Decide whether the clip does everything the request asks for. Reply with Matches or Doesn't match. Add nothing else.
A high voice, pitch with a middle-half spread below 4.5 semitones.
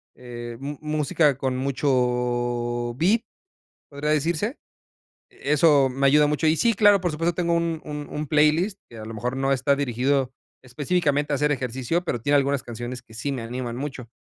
Doesn't match